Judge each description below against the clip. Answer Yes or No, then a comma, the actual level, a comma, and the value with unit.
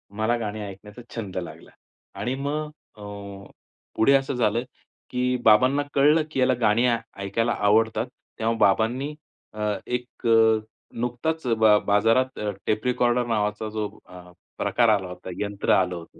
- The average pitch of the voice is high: No, low, 115 Hz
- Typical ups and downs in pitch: Yes, average, 3.1 semitones